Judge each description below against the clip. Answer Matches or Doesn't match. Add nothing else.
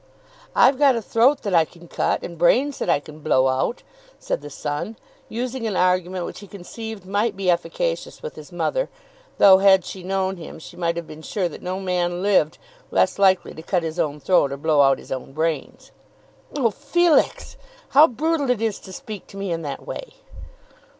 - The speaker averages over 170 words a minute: Matches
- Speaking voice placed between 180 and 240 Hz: Matches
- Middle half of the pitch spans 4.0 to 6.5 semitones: Matches